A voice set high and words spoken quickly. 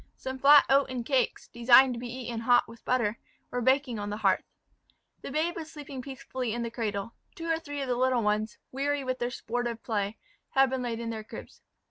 Yes: high, 245 Hz; fast, 215 wpm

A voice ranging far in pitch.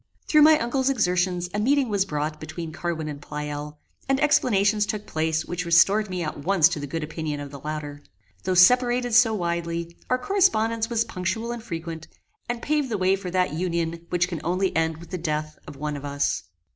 Yes: wide, 5.8 semitones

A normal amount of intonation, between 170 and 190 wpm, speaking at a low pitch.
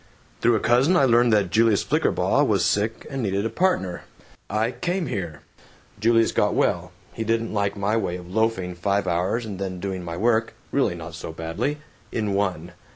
Yes: average, 4.0 semitones; average, 185 wpm; low, 105 Hz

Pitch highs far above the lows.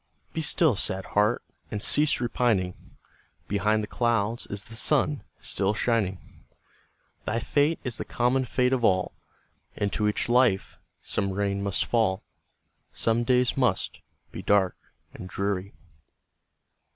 No: average, 3.7 semitones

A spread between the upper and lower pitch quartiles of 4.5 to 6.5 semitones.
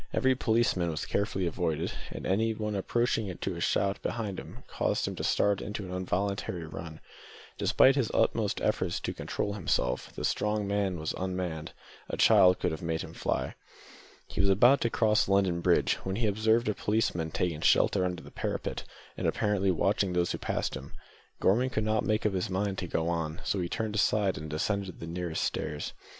No: average, 3.5 semitones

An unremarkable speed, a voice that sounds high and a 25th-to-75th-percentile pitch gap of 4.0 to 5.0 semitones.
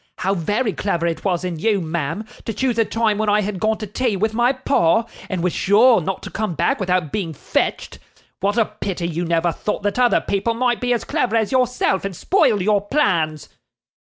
No: fast, 215 wpm; high, 205 Hz; average, 4.3 semitones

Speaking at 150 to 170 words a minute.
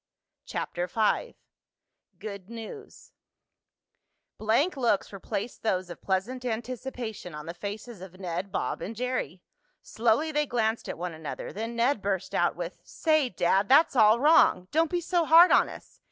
Yes: average, 155 wpm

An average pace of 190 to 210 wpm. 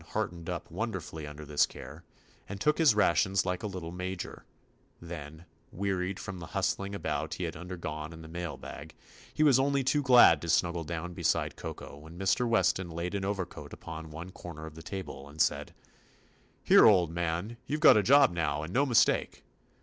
Yes: average, 200 wpm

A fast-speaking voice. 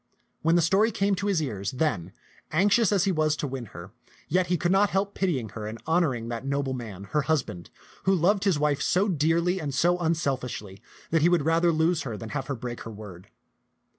Yes: fast, 220 wpm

